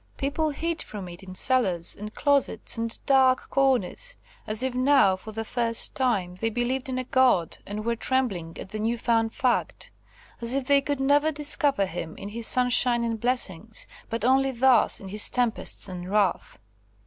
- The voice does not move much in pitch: No, average, 4.0 semitones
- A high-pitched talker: Yes, high, 240 Hz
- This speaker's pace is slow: No, average, 175 wpm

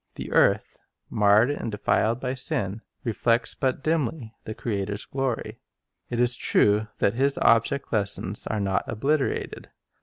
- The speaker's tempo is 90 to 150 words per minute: Yes, average, 140 wpm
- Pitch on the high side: No, low, 115 Hz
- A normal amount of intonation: Yes, average, 4.0 semitones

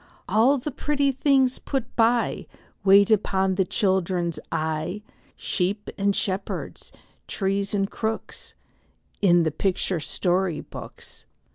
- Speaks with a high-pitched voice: Yes, high, 195 Hz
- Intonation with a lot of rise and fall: No, average, 3.5 semitones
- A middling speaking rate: No, slow, 115 wpm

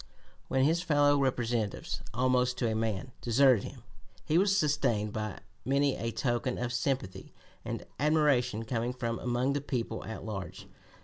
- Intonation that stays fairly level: No, average, 3.5 semitones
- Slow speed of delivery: No, average, 150 wpm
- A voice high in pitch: No, low, 125 Hz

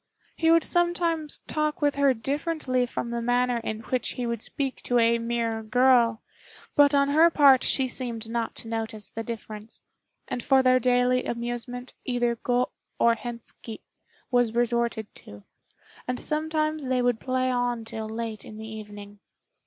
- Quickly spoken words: No, average, 160 wpm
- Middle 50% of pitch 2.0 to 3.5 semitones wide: Yes, narrow, 2.6 semitones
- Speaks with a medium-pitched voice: No, high, 245 Hz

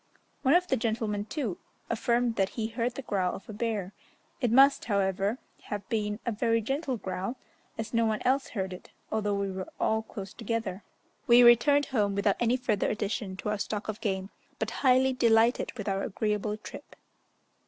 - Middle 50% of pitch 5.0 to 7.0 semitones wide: No, average, 3.1 semitones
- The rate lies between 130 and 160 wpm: No, average, 185 wpm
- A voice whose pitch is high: Yes, high, 220 Hz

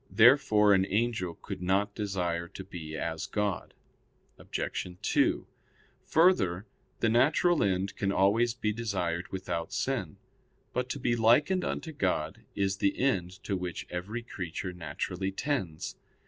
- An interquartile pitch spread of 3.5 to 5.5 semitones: Yes, average, 4.6 semitones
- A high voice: No, low, 100 Hz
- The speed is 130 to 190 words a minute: Yes, slow, 135 wpm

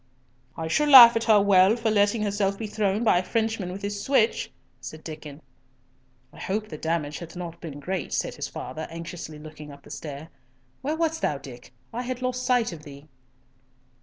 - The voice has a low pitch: No, high, 190 Hz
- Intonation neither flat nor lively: No, wide, 6.2 semitones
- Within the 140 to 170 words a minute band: No, average, 195 wpm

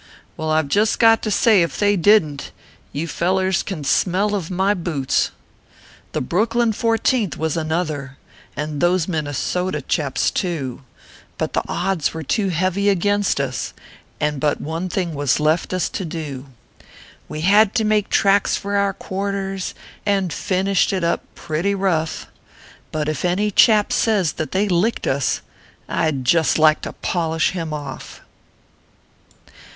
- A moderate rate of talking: Yes, average, 155 wpm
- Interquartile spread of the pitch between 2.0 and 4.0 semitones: No, average, 4.4 semitones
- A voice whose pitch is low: No, medium, 175 Hz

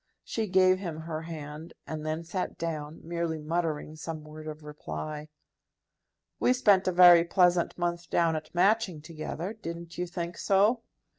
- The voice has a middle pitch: Yes, medium, 170 Hz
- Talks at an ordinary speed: Yes, average, 155 wpm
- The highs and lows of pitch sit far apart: No, narrow, 2.6 semitones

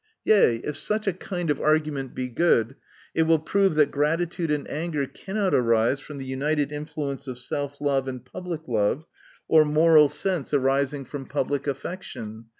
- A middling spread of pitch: Yes, average, 3.3 semitones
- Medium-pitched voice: Yes, medium, 145 Hz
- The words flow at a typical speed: Yes, average, 170 wpm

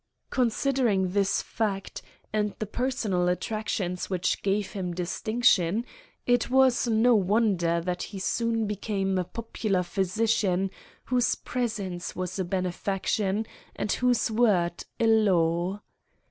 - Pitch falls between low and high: No, high, 200 Hz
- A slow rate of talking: Yes, slow, 120 wpm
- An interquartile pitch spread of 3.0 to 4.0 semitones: Yes, average, 3.7 semitones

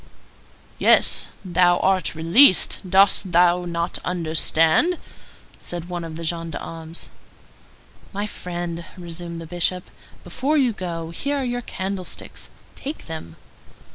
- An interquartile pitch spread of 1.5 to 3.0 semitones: Yes, narrow, 2.4 semitones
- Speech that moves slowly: Yes, slow, 115 wpm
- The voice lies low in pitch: No, medium, 175 Hz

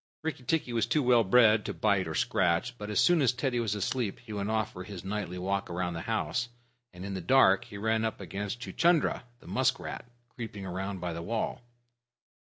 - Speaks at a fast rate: Yes, fast, 210 wpm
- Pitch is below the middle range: Yes, low, 105 Hz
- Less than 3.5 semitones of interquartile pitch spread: No, average, 4.1 semitones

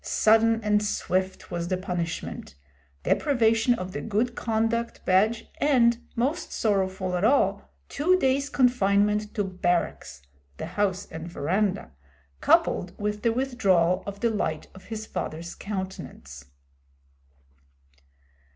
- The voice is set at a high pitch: Yes, high, 205 Hz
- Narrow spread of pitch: No, average, 3.9 semitones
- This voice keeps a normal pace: No, slow, 120 wpm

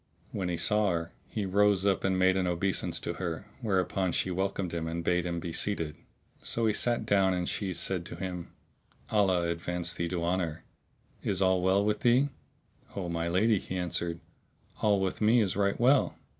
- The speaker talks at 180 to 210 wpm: Yes, average, 190 wpm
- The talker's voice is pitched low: Yes, very low, 95 Hz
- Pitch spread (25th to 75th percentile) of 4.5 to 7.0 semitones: No, narrow, 2.6 semitones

